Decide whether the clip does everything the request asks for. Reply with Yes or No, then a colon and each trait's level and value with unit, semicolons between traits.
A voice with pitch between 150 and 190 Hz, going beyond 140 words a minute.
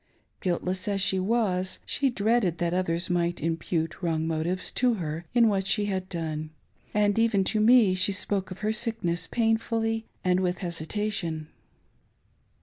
Yes: medium, 185 Hz; average, 155 wpm